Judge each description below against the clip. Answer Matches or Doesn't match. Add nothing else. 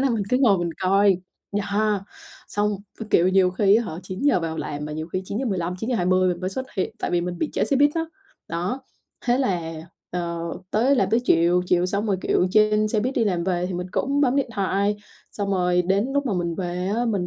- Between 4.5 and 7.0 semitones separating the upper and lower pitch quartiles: Doesn't match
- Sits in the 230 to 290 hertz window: Doesn't match